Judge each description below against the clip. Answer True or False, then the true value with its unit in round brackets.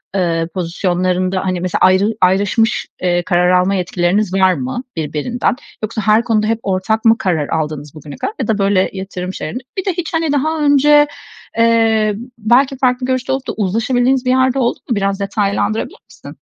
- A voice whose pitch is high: True (205 Hz)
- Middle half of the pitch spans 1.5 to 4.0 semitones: False (5.2 semitones)